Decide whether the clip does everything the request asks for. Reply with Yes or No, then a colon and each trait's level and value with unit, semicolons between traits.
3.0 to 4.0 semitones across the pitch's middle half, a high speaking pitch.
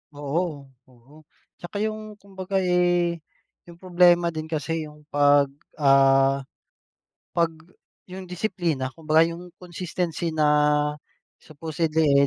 No: average, 3.3 semitones; medium, 165 Hz